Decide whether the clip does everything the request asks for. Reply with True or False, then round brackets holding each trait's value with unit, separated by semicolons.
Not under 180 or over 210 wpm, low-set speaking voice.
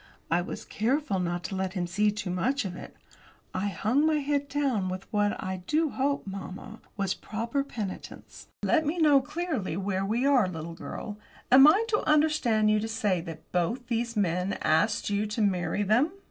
False (190 wpm; 210 Hz)